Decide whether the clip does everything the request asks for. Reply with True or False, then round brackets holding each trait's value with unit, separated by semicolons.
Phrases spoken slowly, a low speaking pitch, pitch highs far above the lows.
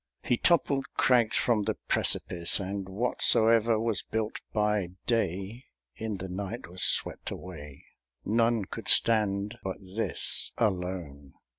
False (110 wpm; 100 Hz; 3.8 semitones)